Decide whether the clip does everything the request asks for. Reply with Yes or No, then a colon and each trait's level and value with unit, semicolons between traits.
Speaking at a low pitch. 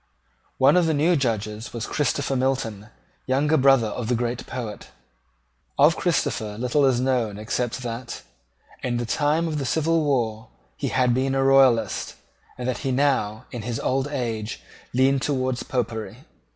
Yes: low, 130 Hz